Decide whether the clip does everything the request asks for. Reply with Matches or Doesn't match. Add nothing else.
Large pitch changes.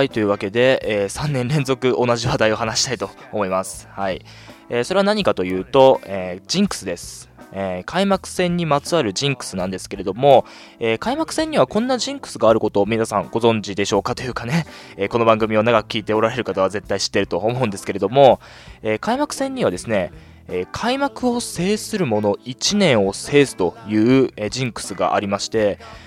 Matches